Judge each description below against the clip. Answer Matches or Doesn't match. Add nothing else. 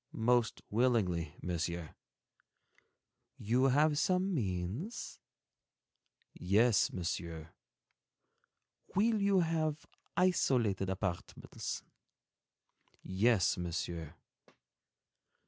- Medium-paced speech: Doesn't match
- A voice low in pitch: Matches